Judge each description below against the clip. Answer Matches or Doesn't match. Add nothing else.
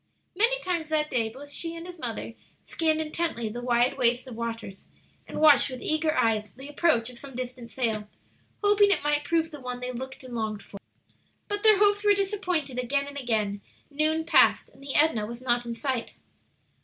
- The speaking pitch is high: Matches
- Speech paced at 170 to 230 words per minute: Matches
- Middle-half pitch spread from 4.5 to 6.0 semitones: Matches